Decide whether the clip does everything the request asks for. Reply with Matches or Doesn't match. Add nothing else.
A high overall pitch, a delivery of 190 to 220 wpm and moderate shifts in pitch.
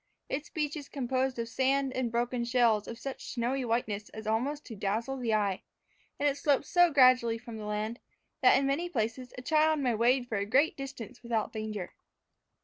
Matches